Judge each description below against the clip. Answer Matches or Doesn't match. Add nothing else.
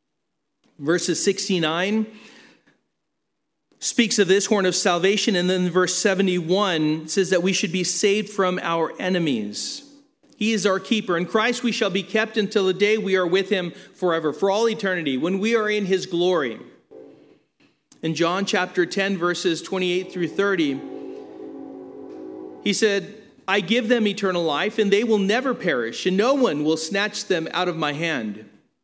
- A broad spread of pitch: Doesn't match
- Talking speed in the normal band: Matches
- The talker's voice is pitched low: Doesn't match